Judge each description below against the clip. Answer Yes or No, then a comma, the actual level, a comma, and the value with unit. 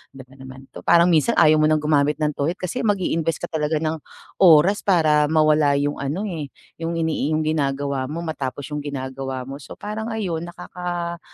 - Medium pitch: Yes, medium, 155 Hz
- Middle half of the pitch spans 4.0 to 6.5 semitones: No, average, 3.1 semitones